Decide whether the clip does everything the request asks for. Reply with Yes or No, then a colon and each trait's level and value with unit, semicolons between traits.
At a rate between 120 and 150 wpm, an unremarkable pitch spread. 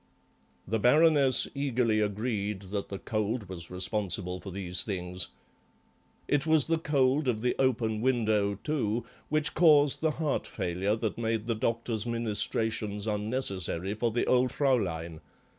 Yes: average, 140 wpm; average, 4.3 semitones